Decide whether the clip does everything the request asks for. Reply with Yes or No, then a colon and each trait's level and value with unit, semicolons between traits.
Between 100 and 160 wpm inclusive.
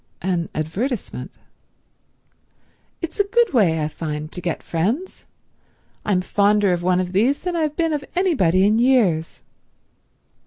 Yes: average, 140 wpm